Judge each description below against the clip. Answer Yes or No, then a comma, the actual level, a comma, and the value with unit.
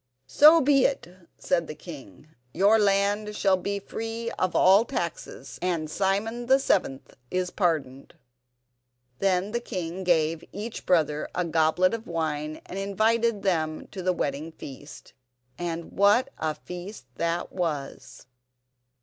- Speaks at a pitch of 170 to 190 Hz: Yes, medium, 185 Hz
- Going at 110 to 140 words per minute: Yes, slow, 135 wpm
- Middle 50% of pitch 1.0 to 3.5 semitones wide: No, average, 4.3 semitones